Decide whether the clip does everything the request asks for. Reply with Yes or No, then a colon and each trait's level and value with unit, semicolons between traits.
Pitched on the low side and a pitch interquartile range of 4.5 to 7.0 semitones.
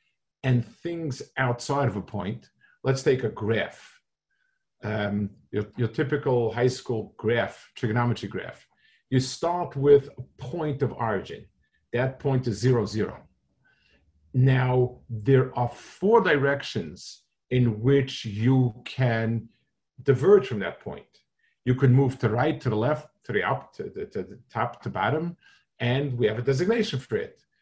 No: low, 130 Hz; average, 3.8 semitones